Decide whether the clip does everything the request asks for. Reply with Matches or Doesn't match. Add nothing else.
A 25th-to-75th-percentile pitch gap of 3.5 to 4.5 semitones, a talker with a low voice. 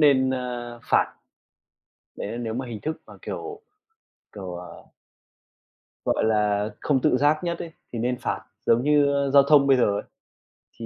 Matches